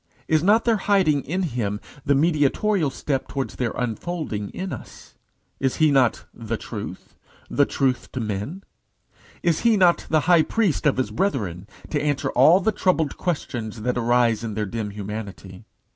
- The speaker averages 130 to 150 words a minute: No, average, 165 wpm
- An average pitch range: No, wide, 7.3 semitones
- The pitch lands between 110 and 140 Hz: Yes, low, 135 Hz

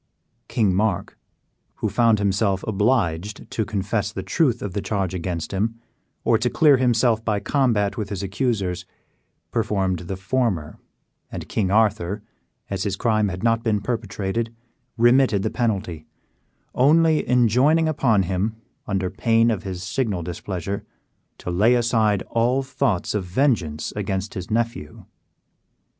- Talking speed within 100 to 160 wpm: Yes, average, 140 wpm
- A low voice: Yes, low, 105 Hz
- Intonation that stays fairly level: No, average, 3.6 semitones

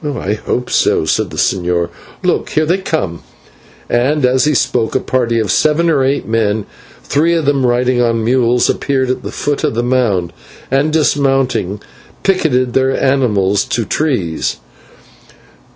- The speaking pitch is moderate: No, low, 125 Hz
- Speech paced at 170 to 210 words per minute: No, average, 155 wpm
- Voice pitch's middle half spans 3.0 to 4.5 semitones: Yes, average, 4.1 semitones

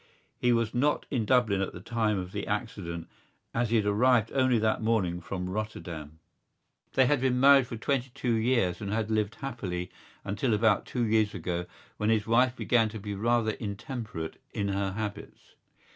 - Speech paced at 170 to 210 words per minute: Yes, average, 180 wpm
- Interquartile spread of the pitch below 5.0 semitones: Yes, average, 3.5 semitones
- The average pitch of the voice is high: No, low, 110 Hz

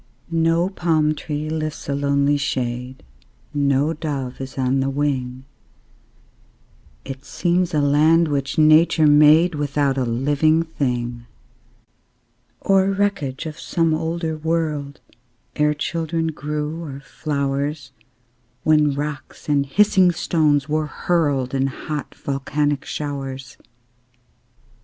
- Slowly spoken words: Yes, slow, 110 wpm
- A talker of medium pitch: Yes, medium, 150 Hz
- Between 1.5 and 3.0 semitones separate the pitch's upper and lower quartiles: Yes, narrow, 2.6 semitones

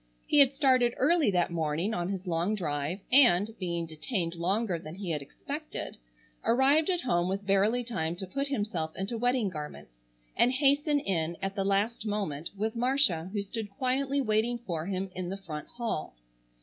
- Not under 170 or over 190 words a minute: Yes, average, 175 wpm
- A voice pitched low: No, high, 200 Hz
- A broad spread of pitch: Yes, wide, 6.1 semitones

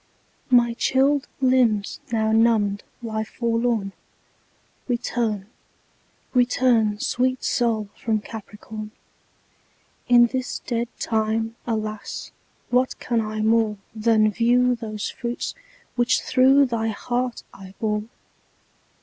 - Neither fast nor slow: No, slow, 100 wpm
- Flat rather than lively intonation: Yes, narrow, 2.2 semitones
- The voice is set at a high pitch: Yes, high, 230 Hz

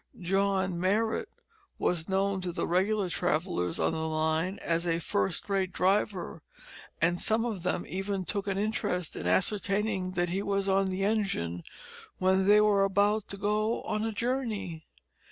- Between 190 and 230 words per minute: No, average, 160 wpm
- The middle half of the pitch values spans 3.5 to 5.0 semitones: No, average, 2.7 semitones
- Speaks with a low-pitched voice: No, high, 190 Hz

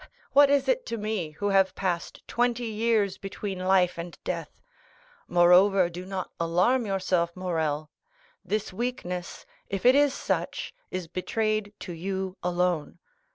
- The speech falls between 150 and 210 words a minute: No, average, 140 wpm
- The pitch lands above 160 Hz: Yes, high, 190 Hz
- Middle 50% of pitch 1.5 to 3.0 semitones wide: No, average, 3.5 semitones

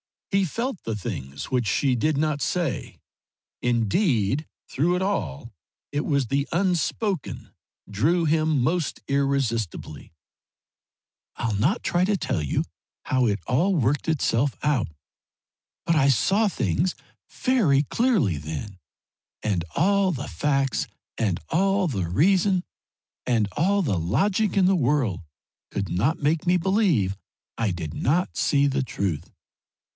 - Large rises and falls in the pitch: Yes, wide, 8.6 semitones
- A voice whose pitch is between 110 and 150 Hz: Yes, medium, 140 Hz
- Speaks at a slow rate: Yes, slow, 130 wpm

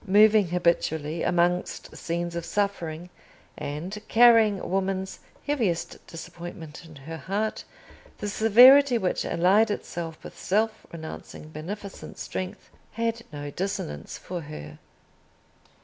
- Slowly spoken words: Yes, slow, 110 wpm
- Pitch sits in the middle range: Yes, medium, 180 Hz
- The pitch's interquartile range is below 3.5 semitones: No, average, 4.3 semitones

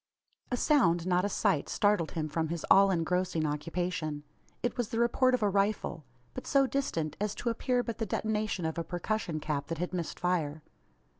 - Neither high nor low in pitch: Yes, medium, 180 Hz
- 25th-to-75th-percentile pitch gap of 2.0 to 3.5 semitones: No, average, 5.1 semitones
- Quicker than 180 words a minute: Yes, average, 195 wpm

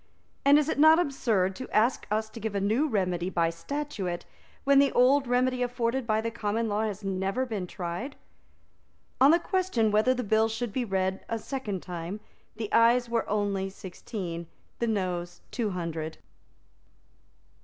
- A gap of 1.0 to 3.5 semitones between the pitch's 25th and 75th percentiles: No, average, 4.8 semitones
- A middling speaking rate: Yes, average, 165 wpm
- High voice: Yes, high, 220 Hz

